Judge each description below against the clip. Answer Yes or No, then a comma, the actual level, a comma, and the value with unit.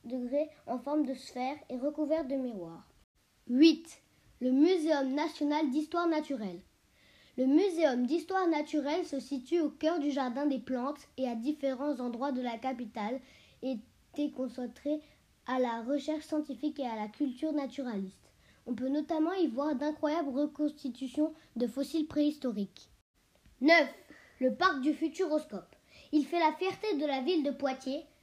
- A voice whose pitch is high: Yes, very high, 290 Hz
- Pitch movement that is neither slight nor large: Yes, average, 3.0 semitones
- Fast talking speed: No, average, 145 wpm